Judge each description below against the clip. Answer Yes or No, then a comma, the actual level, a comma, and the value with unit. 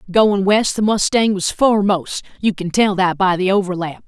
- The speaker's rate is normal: Yes, average, 190 wpm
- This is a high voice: Yes, high, 195 Hz